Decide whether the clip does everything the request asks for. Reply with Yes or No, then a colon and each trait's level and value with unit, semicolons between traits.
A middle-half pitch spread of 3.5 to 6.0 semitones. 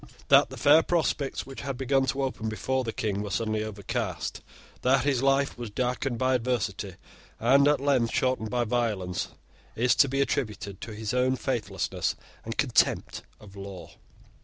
Yes: average, 3.8 semitones